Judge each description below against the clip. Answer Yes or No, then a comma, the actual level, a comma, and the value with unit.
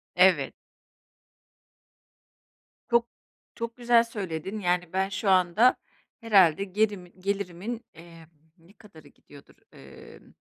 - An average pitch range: Yes, average, 4.0 semitones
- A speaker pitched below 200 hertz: Yes, high, 190 Hz